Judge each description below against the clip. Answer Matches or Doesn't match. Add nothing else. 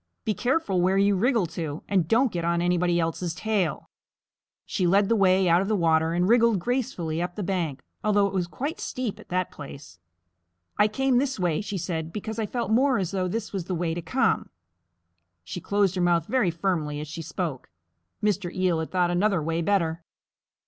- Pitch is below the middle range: Doesn't match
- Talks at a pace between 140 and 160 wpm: Doesn't match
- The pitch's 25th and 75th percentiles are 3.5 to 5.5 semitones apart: Matches